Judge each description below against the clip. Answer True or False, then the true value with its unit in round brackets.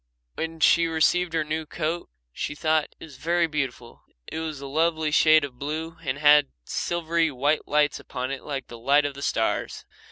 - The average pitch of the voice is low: False (155 Hz)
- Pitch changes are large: False (2.5 semitones)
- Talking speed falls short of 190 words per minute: False (195 wpm)